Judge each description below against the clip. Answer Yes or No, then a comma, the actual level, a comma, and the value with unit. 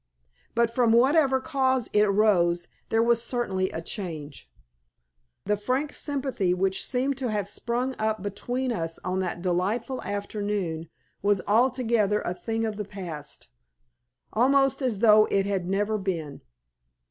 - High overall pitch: Yes, high, 210 Hz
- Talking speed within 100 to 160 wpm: Yes, average, 140 wpm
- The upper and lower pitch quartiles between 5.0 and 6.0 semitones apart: No, average, 4.5 semitones